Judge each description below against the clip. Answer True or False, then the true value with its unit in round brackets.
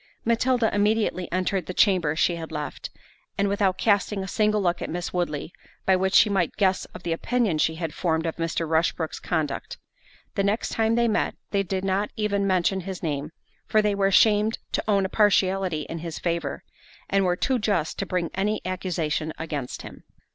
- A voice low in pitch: False (185 Hz)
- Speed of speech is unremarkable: True (190 wpm)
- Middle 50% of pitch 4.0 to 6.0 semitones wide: False (3.6 semitones)